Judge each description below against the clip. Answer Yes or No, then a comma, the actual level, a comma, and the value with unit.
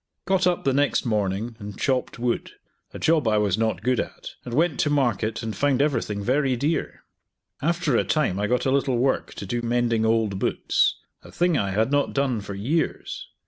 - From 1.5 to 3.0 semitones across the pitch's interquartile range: No, average, 4.7 semitones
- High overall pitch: No, low, 120 Hz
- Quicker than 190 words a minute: Yes, average, 200 wpm